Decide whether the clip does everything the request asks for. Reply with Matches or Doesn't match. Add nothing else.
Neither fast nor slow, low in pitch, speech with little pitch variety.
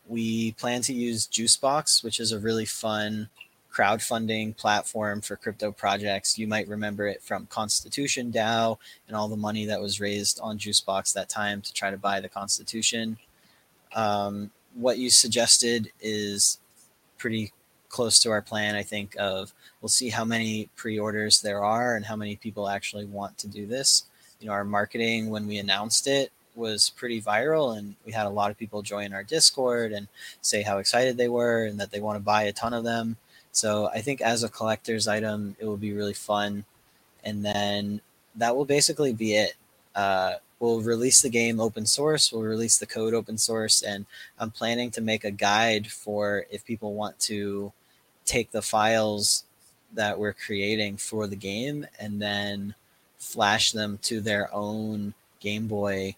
Matches